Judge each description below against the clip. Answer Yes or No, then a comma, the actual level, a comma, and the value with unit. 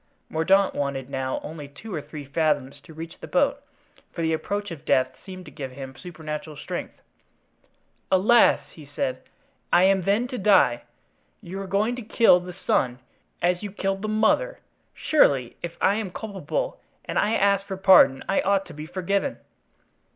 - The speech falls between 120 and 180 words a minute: Yes, average, 175 wpm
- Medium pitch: Yes, medium, 180 Hz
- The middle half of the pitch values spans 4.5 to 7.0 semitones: Yes, average, 5.1 semitones